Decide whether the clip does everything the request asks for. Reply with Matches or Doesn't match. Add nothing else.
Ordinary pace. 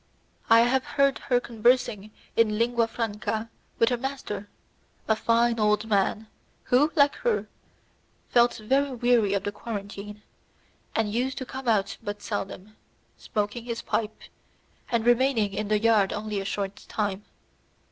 Matches